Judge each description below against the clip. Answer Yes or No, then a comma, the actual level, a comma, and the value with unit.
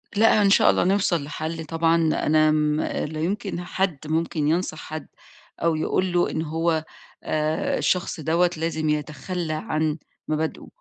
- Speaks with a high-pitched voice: No, medium, 160 Hz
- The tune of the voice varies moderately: No, narrow, 2.0 semitones